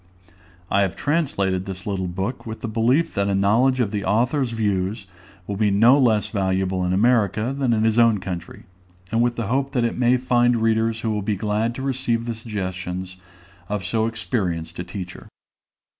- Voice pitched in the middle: No, low, 110 Hz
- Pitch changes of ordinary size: Yes, average, 3.7 semitones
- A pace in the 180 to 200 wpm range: Yes, average, 190 wpm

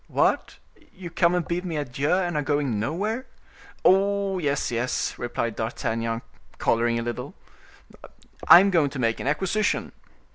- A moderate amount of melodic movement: No, wide, 7.4 semitones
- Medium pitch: Yes, medium, 150 Hz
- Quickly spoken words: No, average, 150 wpm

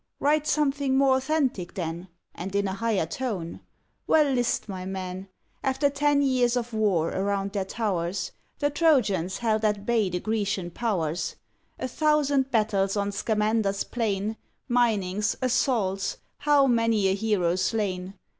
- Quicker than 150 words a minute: No, average, 140 wpm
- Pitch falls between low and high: No, high, 215 Hz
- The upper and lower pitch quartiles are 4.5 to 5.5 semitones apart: Yes, average, 5.1 semitones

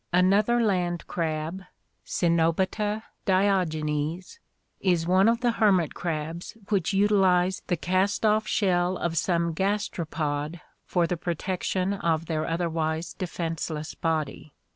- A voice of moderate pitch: Yes, medium, 175 Hz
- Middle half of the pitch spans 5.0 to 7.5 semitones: No, average, 3.0 semitones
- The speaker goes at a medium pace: No, slow, 115 wpm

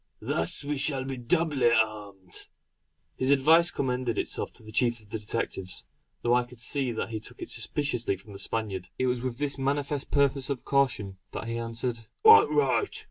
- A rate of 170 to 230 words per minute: Yes, average, 185 wpm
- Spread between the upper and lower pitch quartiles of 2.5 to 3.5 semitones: No, average, 3.9 semitones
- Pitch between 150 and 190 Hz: No, low, 125 Hz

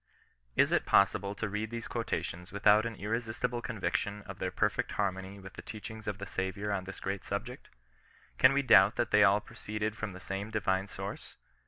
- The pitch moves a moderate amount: No, narrow, 2.1 semitones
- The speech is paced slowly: No, average, 190 wpm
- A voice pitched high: No, low, 105 Hz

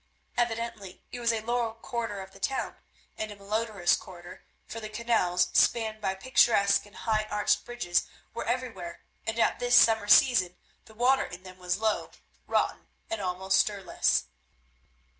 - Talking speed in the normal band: Yes, average, 160 wpm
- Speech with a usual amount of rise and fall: Yes, average, 3.5 semitones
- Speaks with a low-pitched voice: No, high, 215 Hz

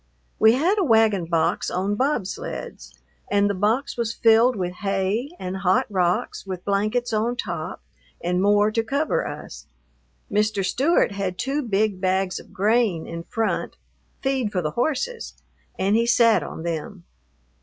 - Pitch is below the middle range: No, high, 210 Hz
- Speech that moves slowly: No, average, 155 wpm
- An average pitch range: Yes, average, 4.1 semitones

